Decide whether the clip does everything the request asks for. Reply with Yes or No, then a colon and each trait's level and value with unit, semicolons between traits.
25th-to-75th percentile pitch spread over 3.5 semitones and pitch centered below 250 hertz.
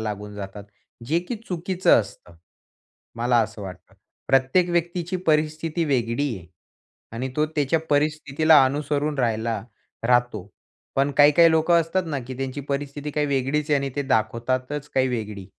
Yes: average, 4.5 semitones; medium, 140 Hz